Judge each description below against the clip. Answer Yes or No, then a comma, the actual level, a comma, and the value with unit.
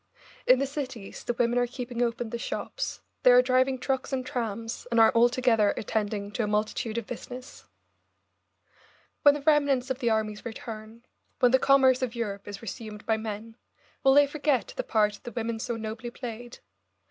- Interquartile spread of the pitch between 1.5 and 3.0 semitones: Yes, narrow, 2.6 semitones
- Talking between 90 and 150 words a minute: No, average, 180 wpm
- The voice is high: Yes, high, 235 Hz